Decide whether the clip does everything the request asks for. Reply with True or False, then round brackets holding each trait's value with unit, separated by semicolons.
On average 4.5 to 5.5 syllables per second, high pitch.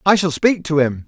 False (5.3 syllables/s; 160 Hz)